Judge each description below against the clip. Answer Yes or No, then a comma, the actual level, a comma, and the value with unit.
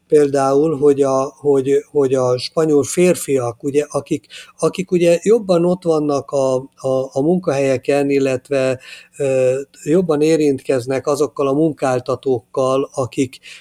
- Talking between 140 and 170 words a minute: No, average, 120 wpm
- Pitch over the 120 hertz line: Yes, medium, 140 Hz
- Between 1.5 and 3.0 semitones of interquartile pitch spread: Yes, narrow, 2.5 semitones